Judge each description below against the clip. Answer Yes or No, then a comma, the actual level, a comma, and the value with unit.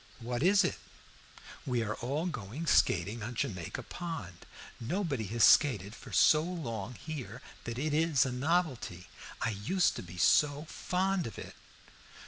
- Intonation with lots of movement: Yes, wide, 6.7 semitones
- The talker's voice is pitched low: Yes, low, 125 Hz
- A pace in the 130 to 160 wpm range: Yes, average, 150 wpm